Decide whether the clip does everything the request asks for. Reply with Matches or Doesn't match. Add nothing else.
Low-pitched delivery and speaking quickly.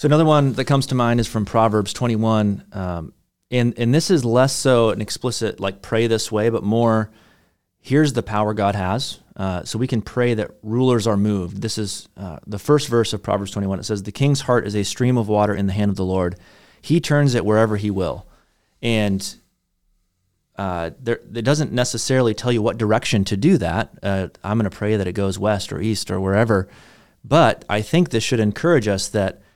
Matches